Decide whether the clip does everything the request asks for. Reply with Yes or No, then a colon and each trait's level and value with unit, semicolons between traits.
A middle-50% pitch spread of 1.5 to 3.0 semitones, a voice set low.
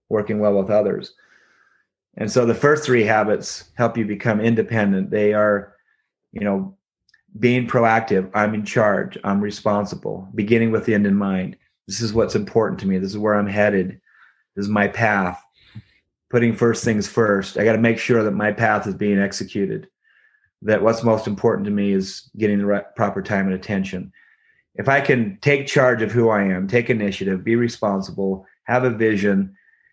Yes: narrow, 2.6 semitones; low, 105 Hz